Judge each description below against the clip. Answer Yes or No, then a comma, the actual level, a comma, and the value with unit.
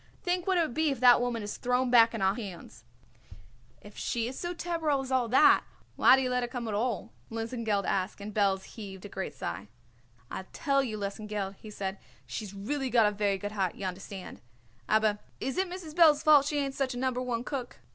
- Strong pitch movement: No, average, 4.8 semitones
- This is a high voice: Yes, high, 235 Hz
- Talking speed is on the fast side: Yes, fast, 220 wpm